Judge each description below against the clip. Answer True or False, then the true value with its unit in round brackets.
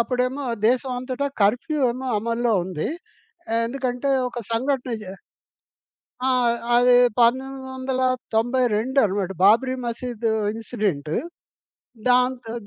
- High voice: True (245 Hz)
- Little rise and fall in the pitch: True (2.2 semitones)